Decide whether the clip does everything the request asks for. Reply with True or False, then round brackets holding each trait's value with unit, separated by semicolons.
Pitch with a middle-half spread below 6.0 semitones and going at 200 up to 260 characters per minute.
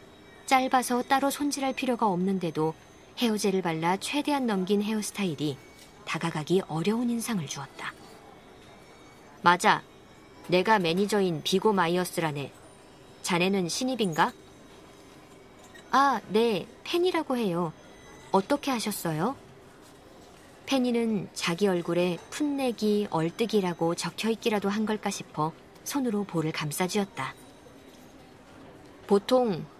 True (5.5 semitones; 245 characters per minute)